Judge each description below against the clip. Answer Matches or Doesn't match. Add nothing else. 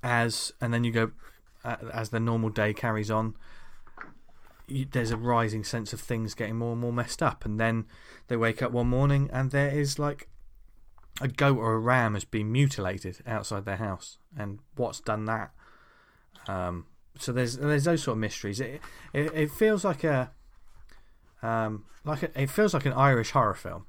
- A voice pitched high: Doesn't match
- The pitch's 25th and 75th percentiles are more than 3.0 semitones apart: Matches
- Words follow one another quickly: Doesn't match